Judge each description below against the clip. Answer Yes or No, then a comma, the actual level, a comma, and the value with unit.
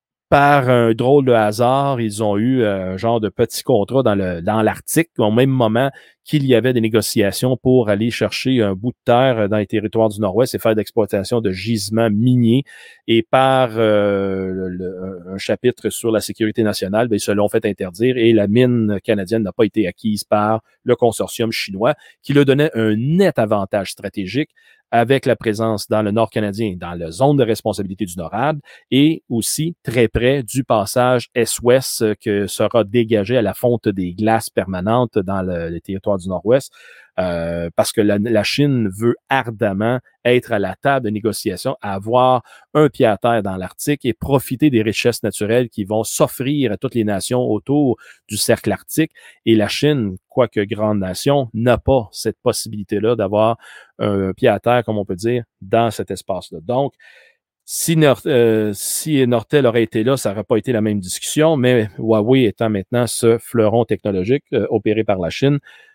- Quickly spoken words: No, average, 180 wpm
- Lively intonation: No, average, 3.4 semitones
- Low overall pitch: Yes, low, 115 Hz